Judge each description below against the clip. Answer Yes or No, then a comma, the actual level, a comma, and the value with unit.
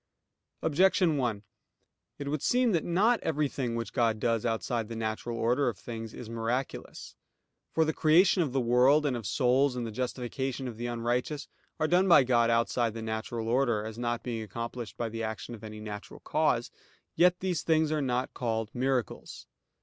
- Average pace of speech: Yes, average, 180 wpm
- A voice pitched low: Yes, low, 120 Hz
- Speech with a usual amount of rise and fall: Yes, average, 4.1 semitones